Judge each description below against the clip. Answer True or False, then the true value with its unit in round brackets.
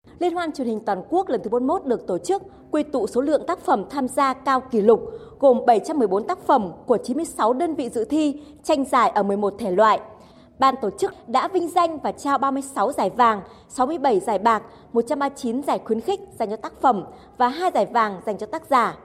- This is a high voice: True (265 Hz)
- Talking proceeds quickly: False (215 wpm)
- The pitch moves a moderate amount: False (6.2 semitones)